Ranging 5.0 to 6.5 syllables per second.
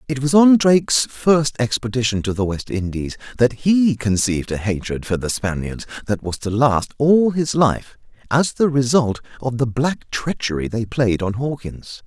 No: 4.5 syllables/s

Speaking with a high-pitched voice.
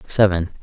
No: very low, 95 Hz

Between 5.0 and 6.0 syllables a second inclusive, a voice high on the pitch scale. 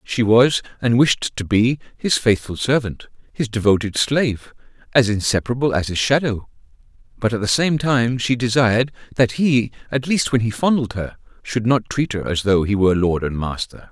No: 5.1 syllables/s; low, 115 Hz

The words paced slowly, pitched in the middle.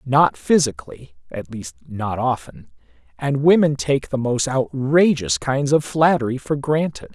No: slow, 125 wpm; low, 130 Hz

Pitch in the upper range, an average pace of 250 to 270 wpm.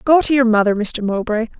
No: high, 230 Hz; fast, 225 wpm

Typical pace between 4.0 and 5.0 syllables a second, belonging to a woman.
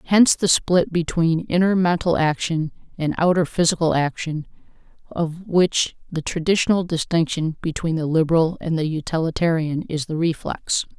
Yes: 4.9 syllables/s; female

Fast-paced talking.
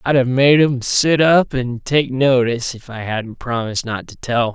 Yes: fast, 210 wpm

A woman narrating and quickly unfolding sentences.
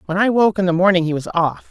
Yes: female; fast, 315 wpm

